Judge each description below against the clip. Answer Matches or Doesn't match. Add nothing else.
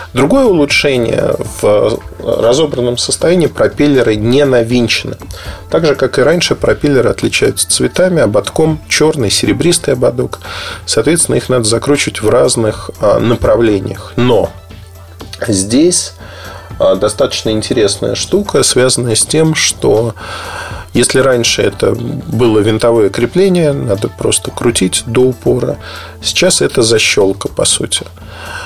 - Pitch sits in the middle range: Doesn't match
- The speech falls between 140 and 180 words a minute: Doesn't match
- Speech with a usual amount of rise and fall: Doesn't match